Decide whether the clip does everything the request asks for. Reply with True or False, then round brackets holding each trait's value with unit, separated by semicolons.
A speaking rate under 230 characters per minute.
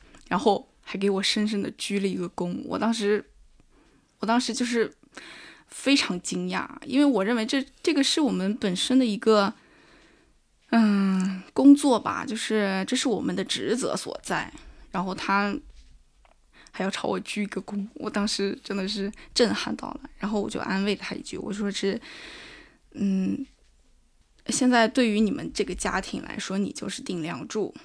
False (235 characters per minute)